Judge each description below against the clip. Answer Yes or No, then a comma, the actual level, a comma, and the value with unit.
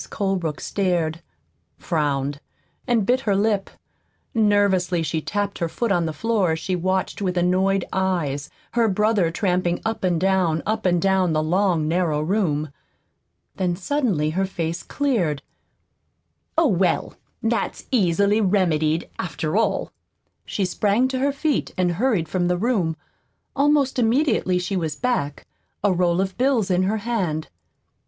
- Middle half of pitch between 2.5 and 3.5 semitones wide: No, average, 4.2 semitones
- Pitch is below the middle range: No, medium, 185 Hz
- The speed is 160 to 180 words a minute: No, average, 145 wpm